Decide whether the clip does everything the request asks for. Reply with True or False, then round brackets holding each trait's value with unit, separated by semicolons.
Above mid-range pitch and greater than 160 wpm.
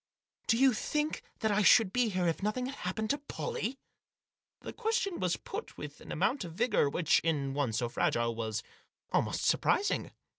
True (210 Hz; 180 wpm)